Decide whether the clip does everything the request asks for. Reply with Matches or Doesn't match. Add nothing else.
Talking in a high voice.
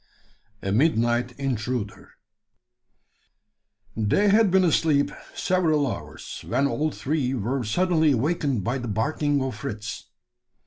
Doesn't match